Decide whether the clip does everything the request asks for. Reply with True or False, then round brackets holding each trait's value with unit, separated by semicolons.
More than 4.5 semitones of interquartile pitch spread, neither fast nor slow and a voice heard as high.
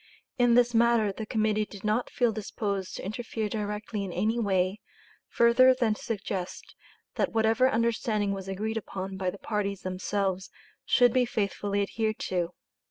False (2.6 semitones; 160 wpm; 215 Hz)